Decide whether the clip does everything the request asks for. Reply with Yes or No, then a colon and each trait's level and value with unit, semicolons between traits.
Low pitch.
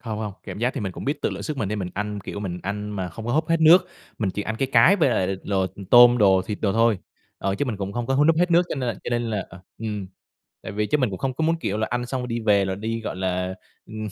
Yes: low, 110 Hz